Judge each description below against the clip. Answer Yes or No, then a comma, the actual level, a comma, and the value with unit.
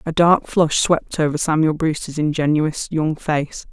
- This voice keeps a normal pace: Yes, average, 160 wpm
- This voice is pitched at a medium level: Yes, medium, 155 Hz